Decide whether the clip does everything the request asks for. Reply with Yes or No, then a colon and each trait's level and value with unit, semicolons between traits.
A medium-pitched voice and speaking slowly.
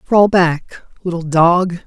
Yes: medium, 175 Hz; slow, 130 wpm